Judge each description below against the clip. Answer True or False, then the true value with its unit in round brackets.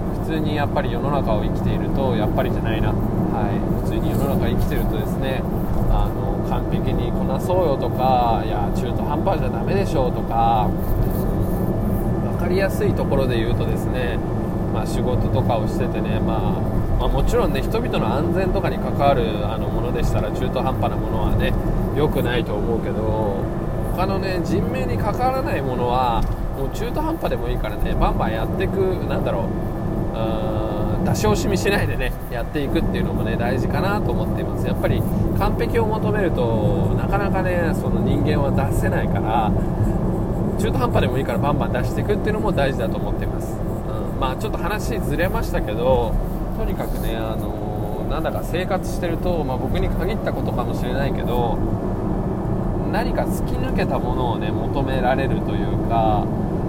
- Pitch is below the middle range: True (110 Hz)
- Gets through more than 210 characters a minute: True (375 characters per minute)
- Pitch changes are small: True (1.1 semitones)